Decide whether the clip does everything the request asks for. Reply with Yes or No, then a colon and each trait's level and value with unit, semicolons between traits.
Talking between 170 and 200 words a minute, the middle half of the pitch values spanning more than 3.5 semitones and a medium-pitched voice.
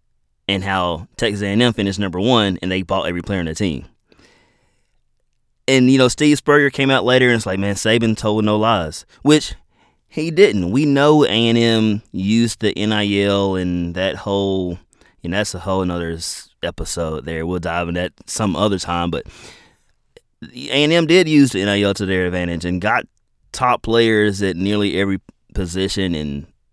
No: average, 175 wpm; average, 4.5 semitones; low, 100 Hz